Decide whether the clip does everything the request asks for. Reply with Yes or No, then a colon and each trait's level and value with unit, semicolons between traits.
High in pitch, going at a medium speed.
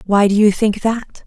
No: high, 210 Hz; fast, 235 wpm